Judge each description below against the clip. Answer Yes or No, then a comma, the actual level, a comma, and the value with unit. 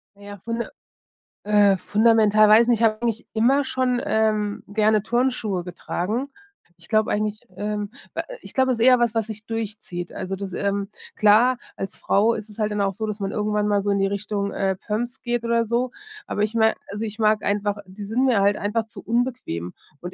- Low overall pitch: No, high, 215 Hz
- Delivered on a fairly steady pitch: Yes, narrow, 2.3 semitones